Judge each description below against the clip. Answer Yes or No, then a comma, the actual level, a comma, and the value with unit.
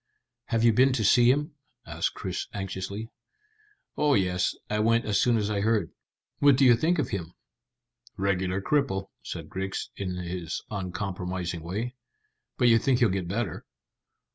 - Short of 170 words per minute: Yes, average, 160 wpm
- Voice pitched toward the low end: Yes, low, 100 Hz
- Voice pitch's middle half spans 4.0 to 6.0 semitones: Yes, average, 4.4 semitones